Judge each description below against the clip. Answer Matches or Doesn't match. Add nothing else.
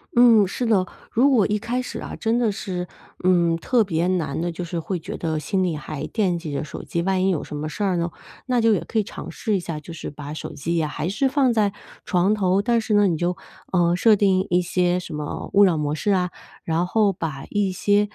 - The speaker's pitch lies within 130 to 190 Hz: Matches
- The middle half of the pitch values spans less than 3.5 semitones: Doesn't match